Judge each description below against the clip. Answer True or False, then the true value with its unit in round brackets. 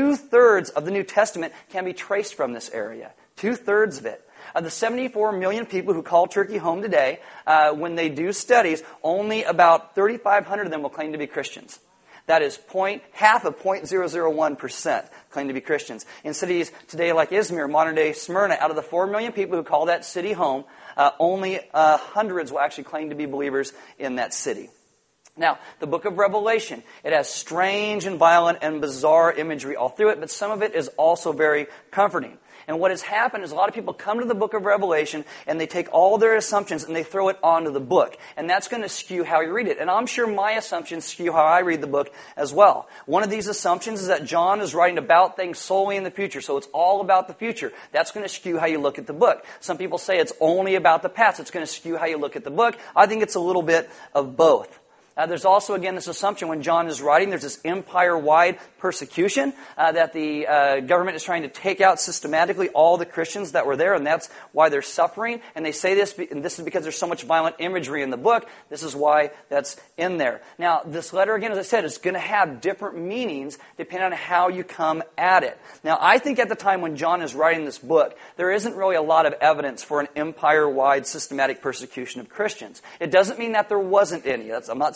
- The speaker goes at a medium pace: False (230 wpm)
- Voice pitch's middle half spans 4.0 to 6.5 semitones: True (4.4 semitones)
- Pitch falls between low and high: True (175 Hz)